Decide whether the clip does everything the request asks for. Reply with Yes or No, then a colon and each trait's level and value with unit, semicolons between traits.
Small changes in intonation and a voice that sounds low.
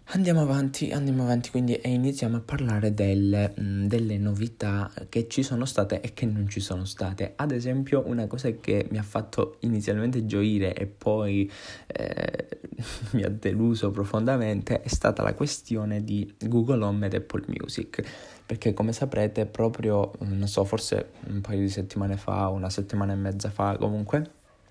No: average, 3.1 semitones; low, 105 Hz